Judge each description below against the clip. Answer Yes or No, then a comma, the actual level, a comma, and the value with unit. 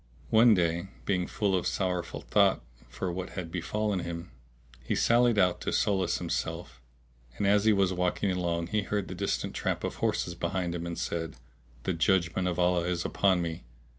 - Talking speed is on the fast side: No, average, 180 wpm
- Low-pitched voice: Yes, very low, 90 Hz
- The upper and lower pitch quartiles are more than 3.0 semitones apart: No, narrow, 2.5 semitones